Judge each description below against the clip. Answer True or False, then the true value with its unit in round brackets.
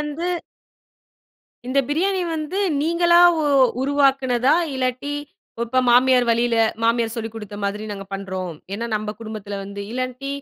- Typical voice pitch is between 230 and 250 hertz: True (245 Hz)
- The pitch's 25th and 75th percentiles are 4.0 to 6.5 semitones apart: True (4.7 semitones)